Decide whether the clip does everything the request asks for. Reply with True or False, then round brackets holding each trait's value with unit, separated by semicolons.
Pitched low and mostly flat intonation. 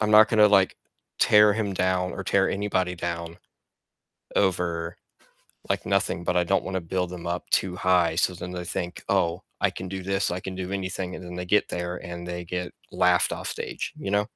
True (90 Hz; 1.6 semitones)